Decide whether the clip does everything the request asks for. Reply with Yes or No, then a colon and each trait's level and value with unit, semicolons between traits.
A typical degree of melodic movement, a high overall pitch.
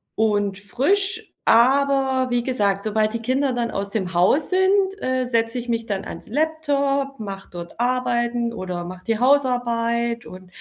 Yes: average, 4.2 semitones; high, 235 Hz